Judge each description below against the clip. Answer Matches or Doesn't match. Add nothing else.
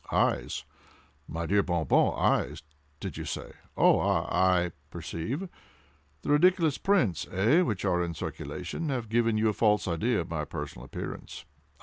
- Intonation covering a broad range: Matches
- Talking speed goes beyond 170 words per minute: Doesn't match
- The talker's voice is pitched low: Matches